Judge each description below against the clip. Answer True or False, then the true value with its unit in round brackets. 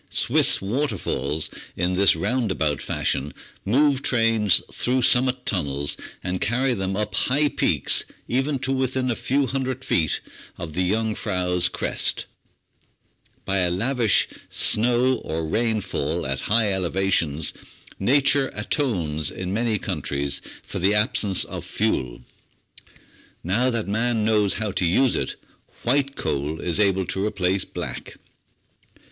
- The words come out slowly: True (130 wpm)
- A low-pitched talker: True (105 Hz)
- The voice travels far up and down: True (5.9 semitones)